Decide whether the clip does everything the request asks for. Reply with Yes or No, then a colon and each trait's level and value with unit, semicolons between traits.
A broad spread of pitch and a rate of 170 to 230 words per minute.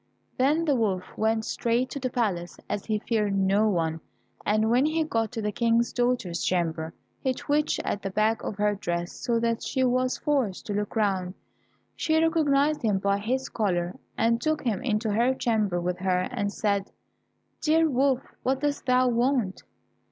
No: average, 4.5 semitones; average, 180 wpm